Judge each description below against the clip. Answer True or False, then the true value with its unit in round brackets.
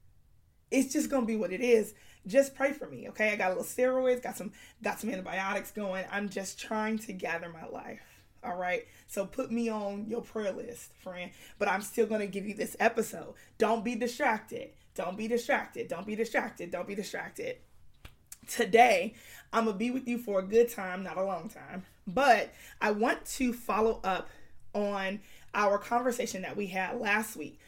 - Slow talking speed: False (190 wpm)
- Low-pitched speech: False (220 Hz)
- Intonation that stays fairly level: False (3.8 semitones)